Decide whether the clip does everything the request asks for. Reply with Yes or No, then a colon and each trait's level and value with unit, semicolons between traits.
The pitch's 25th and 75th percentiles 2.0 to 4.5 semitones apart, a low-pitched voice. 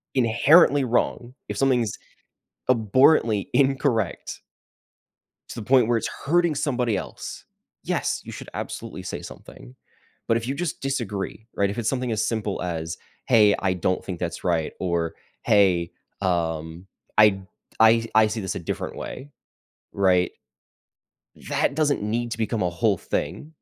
No: average, 5.2 semitones; low, 110 Hz